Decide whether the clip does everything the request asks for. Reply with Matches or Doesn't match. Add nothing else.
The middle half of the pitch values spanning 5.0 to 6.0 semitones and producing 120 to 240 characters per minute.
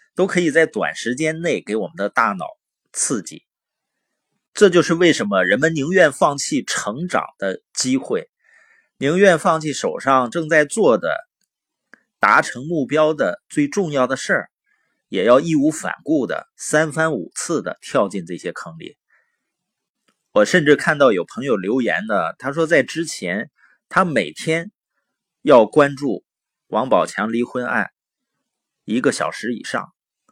Matches